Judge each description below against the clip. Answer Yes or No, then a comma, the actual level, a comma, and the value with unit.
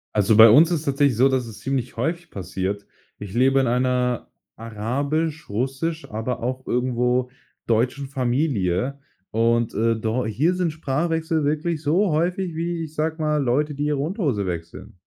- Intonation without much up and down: No, average, 5.3 semitones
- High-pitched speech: No, low, 130 Hz